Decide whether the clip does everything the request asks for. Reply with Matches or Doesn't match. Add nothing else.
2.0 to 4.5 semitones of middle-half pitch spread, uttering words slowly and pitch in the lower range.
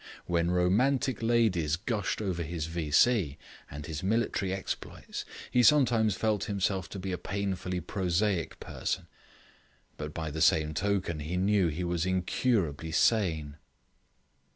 Matches